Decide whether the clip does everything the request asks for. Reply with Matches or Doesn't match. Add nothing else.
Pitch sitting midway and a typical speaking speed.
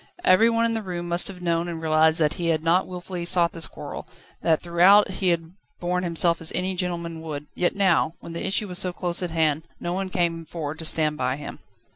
Doesn't match